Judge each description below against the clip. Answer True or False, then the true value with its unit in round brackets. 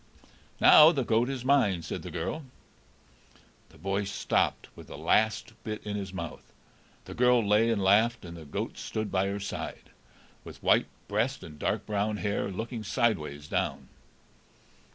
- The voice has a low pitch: True (105 Hz)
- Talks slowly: False (160 wpm)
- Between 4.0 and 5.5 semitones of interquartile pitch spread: False (3.2 semitones)